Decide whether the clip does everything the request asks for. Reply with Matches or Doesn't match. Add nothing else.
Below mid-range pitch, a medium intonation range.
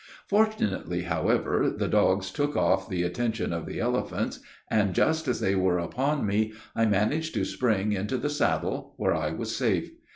Doesn't match